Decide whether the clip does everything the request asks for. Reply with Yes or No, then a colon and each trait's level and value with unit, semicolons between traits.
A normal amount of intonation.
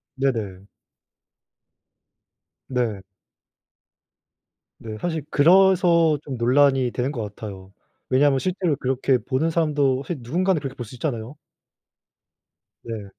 Yes: average, 5.0 semitones